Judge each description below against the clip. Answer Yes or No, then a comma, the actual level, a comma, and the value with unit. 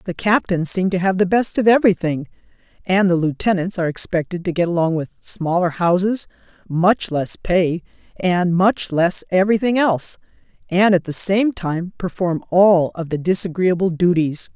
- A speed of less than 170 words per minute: Yes, average, 160 wpm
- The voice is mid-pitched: Yes, medium, 180 Hz